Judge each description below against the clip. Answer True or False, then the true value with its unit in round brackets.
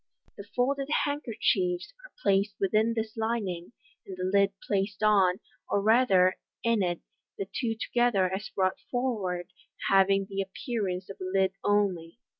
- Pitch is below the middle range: False (200 Hz)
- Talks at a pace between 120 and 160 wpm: True (150 wpm)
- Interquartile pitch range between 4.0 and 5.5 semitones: False (3.3 semitones)